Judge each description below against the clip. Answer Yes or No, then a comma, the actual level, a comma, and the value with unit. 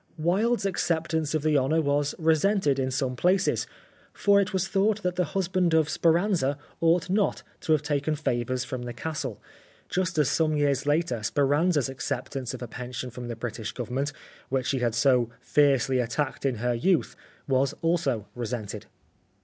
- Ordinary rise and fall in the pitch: Yes, average, 4.9 semitones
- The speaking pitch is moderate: Yes, medium, 145 Hz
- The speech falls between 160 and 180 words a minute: Yes, average, 170 wpm